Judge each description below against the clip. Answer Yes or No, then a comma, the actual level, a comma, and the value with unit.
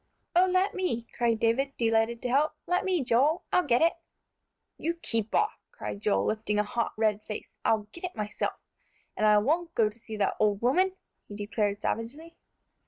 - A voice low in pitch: No, high, 235 Hz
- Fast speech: No, average, 185 wpm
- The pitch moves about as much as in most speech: No, wide, 7.5 semitones